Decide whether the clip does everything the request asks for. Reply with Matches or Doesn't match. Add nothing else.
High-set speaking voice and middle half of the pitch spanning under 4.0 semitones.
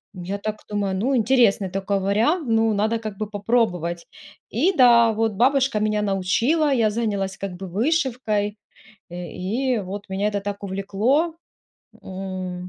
Matches